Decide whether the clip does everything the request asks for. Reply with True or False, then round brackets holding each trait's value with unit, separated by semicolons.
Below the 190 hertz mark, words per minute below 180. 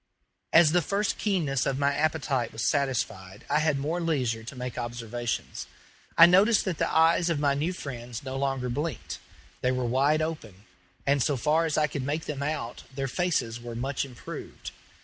False (140 Hz; 185 wpm)